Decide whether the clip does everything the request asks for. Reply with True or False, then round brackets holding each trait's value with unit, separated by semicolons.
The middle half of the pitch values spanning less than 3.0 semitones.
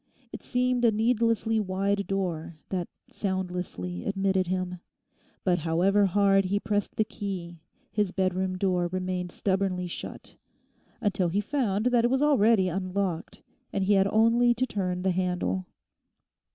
True (2.5 semitones)